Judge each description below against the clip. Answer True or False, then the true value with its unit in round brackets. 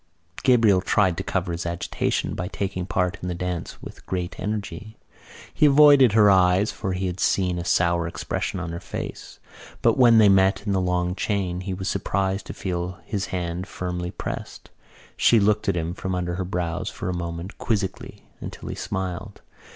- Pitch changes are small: True (2.1 semitones)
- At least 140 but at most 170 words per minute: False (185 wpm)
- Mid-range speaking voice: False (95 Hz)